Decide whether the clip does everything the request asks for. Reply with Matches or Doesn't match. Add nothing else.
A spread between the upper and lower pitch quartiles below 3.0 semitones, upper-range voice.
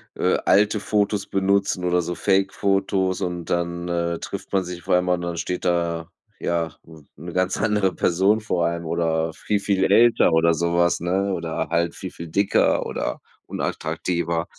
Doesn't match